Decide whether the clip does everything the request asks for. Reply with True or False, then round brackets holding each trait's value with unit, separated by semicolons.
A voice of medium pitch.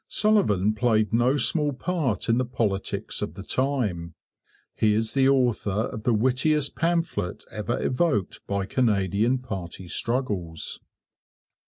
False (115 Hz)